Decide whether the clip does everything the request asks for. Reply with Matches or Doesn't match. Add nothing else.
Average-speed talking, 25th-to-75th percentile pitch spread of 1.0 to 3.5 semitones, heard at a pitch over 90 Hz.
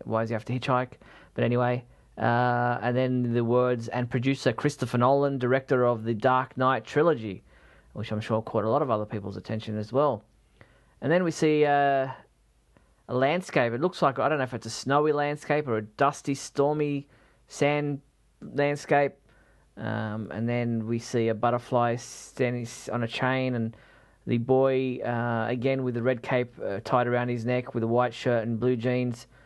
Matches